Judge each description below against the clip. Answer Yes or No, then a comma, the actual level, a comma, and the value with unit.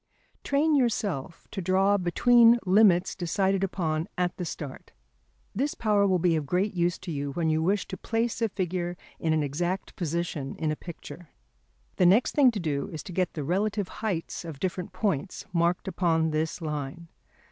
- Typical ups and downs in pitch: Yes, average, 3.7 semitones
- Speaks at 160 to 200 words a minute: Yes, average, 180 wpm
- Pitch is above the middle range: No, medium, 180 Hz